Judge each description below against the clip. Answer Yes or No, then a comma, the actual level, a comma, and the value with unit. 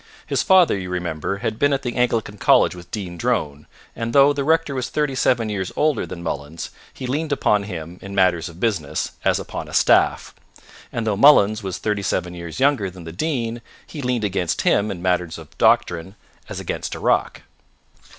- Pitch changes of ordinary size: No, wide, 6.3 semitones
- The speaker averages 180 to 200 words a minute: Yes, average, 195 wpm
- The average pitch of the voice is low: Yes, low, 100 Hz